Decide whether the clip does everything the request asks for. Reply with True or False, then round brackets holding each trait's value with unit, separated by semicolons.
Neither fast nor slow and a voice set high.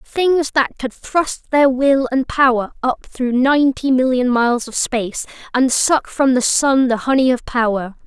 True (180 wpm; 260 Hz)